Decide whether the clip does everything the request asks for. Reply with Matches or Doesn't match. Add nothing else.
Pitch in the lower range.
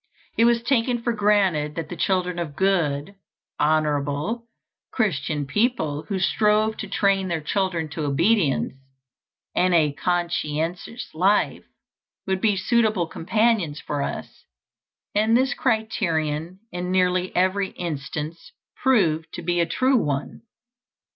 Doesn't match